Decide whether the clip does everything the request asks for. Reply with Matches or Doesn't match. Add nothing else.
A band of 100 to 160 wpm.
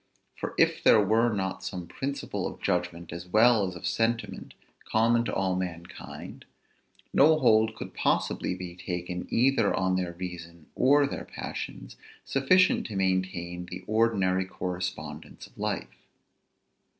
Matches